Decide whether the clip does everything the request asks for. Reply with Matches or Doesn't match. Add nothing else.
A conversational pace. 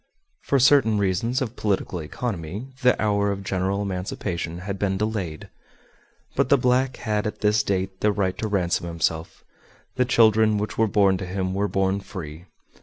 Matches